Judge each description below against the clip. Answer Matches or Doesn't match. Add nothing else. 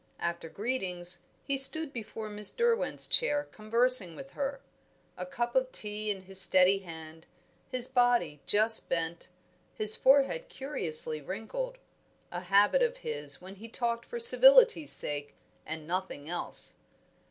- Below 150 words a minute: Matches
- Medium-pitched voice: Doesn't match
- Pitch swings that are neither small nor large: Doesn't match